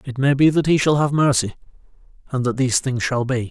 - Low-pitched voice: Yes, low, 130 Hz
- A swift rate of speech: Yes, fast, 240 wpm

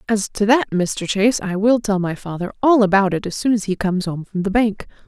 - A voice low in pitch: No, high, 205 Hz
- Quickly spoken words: Yes, fast, 260 wpm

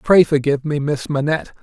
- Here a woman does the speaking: No, male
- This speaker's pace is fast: No, average, 185 wpm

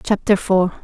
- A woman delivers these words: Yes, female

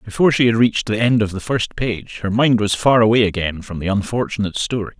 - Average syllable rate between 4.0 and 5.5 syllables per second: No, 6.2 syllables/s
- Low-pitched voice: Yes, low, 110 Hz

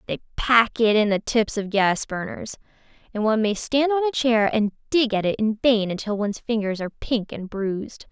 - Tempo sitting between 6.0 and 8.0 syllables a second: No, 5.4 syllables/s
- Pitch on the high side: Yes, high, 220 Hz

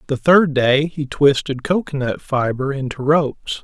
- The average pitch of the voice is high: No, medium, 140 Hz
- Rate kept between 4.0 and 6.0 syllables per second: Yes, 4.4 syllables/s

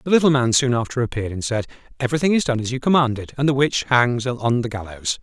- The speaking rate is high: Yes, fast, 240 wpm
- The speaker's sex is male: Yes, male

